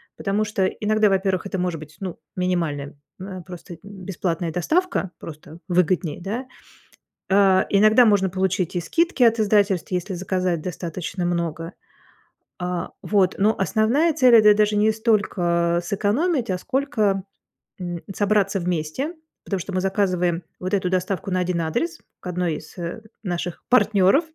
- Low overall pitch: No, high, 190 Hz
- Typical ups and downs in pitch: Yes, average, 3.2 semitones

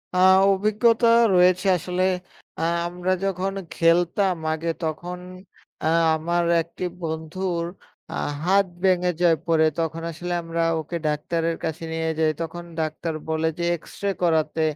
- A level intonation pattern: Yes, narrow, 2.0 semitones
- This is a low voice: No, medium, 170 Hz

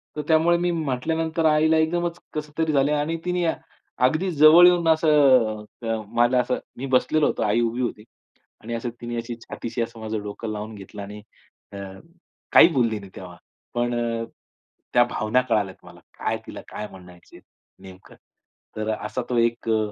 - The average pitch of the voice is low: Yes, low, 120 Hz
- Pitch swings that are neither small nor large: No, wide, 6.3 semitones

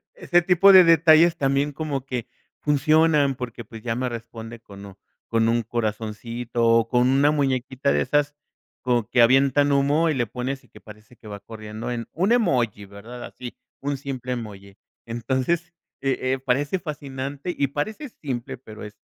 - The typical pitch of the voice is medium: No, low, 130 Hz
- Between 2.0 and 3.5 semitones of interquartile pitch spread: No, average, 4.0 semitones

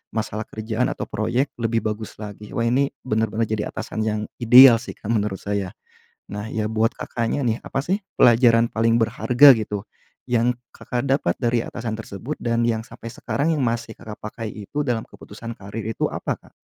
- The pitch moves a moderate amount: No, narrow, 2.0 semitones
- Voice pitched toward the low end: Yes, low, 115 Hz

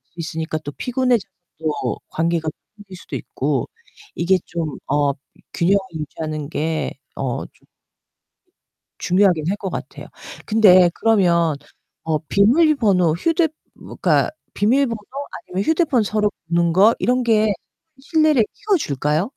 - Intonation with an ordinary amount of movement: No, wide, 6.0 semitones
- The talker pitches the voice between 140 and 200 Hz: Yes, high, 190 Hz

